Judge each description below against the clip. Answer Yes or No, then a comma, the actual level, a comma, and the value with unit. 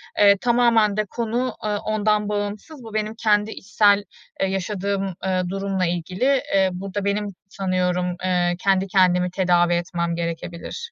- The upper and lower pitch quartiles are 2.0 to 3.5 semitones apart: Yes, narrow, 2.6 semitones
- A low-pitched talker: No, high, 195 Hz